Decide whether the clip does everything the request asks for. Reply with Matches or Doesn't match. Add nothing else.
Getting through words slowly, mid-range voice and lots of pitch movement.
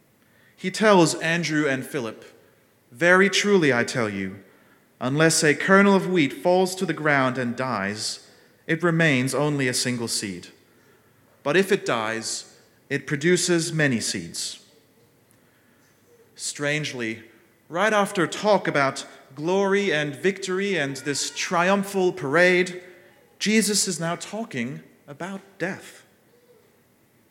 Matches